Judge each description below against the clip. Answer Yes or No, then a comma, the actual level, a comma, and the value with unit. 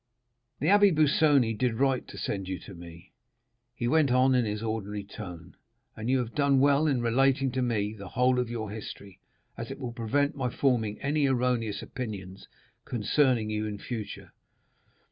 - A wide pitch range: No, average, 4.2 semitones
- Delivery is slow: No, average, 175 wpm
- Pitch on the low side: Yes, low, 120 Hz